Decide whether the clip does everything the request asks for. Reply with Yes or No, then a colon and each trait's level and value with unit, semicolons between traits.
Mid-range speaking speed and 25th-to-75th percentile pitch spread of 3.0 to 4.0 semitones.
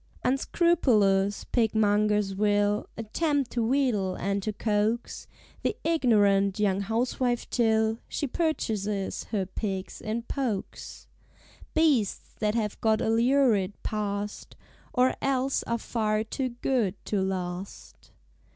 No: slow, 115 wpm; average, 3.4 semitones